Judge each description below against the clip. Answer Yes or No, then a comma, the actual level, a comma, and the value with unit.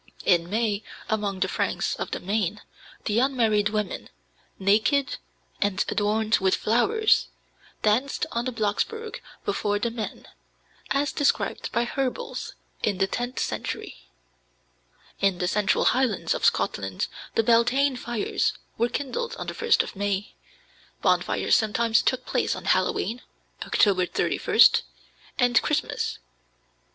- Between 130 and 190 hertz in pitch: No, high, 220 Hz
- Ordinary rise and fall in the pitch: Yes, average, 3.6 semitones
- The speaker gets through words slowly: Yes, slow, 125 wpm